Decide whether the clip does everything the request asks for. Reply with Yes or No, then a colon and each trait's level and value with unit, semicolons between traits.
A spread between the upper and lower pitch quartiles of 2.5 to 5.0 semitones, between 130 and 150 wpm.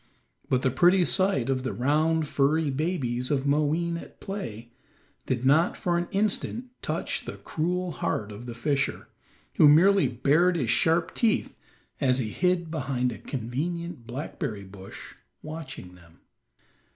No: wide, 5.4 semitones; average, 145 wpm